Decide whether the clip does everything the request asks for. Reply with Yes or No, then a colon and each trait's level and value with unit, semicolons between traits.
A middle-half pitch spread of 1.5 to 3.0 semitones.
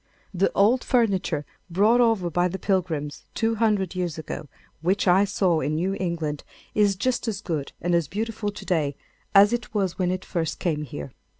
No: average, 4.0 semitones